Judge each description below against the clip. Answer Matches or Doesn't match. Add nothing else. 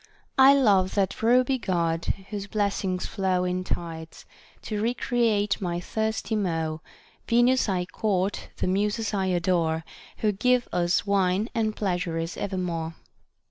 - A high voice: Matches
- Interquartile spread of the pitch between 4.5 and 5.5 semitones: Doesn't match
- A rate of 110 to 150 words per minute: Matches